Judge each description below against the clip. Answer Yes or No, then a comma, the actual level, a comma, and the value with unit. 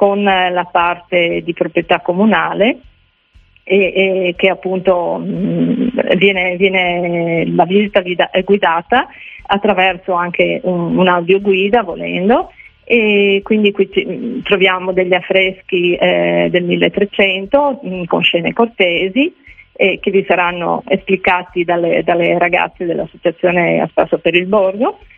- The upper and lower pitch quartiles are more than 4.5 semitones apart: No, narrow, 2.4 semitones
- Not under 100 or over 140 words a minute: Yes, average, 120 wpm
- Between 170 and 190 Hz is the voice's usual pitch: Yes, medium, 185 Hz